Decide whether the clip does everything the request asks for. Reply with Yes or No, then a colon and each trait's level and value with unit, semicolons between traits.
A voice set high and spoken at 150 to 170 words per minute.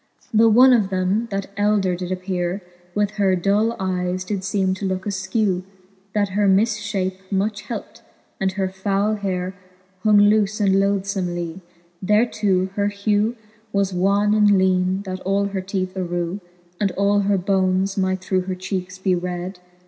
Yes: high, 195 Hz; average, 165 wpm